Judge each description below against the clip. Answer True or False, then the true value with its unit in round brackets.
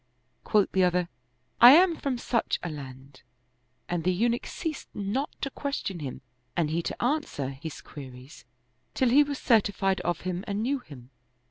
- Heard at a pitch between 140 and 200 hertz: True (190 Hz)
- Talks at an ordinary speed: True (170 wpm)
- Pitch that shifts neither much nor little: False (8.8 semitones)